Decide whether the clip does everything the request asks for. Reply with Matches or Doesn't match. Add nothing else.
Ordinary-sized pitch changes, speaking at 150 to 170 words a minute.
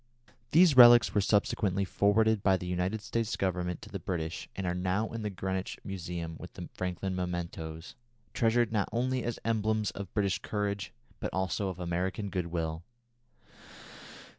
Matches